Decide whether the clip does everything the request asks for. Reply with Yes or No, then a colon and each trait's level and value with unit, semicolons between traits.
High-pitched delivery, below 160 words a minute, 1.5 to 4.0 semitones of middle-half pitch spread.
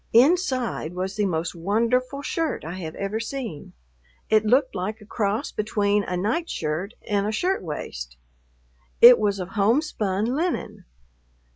No: high, 210 Hz; average, 140 wpm; average, 5.0 semitones